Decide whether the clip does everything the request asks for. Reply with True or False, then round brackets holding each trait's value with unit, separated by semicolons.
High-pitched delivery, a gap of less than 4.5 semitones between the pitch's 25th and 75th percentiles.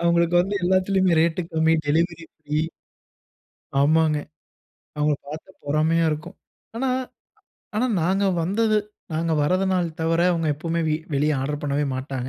False (165 Hz; 3.0 semitones)